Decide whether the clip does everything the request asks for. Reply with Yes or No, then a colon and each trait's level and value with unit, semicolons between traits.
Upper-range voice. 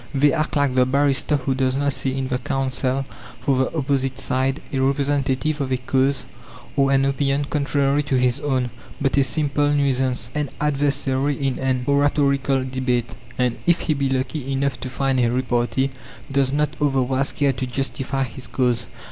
No: low, 135 Hz